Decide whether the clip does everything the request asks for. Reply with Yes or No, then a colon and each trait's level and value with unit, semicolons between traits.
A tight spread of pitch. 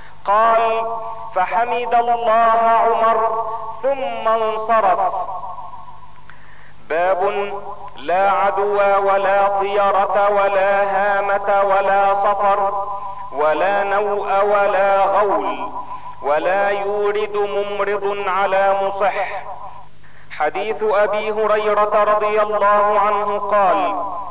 Yes: narrow, 2.0 semitones